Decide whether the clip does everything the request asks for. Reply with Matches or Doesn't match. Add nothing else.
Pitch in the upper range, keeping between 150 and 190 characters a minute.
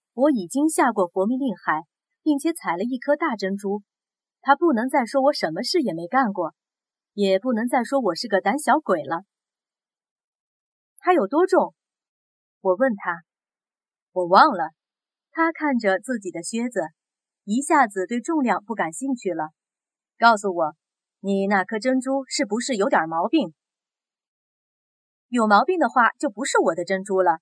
Doesn't match